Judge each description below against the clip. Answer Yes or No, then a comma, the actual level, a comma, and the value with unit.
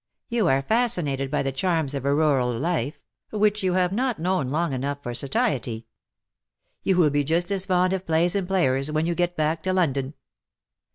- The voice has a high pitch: No, medium, 160 Hz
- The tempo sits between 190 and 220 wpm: Yes, average, 195 wpm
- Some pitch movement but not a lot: Yes, average, 5.0 semitones